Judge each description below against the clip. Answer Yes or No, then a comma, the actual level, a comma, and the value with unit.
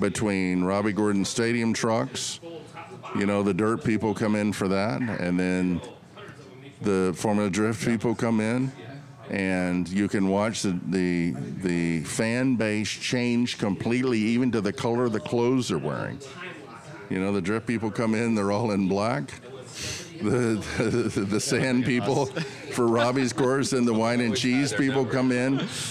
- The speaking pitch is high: No, low, 115 Hz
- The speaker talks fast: No, average, 160 wpm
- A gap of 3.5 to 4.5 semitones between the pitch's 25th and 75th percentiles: Yes, average, 3.8 semitones